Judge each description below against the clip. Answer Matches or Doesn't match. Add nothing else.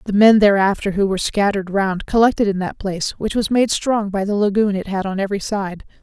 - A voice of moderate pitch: Doesn't match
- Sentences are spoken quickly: Matches